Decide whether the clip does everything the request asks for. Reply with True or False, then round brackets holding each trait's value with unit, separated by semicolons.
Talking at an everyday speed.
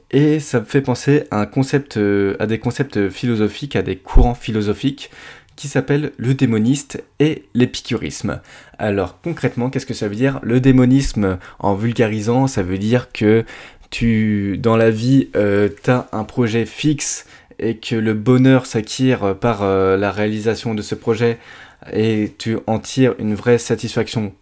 True (160 wpm)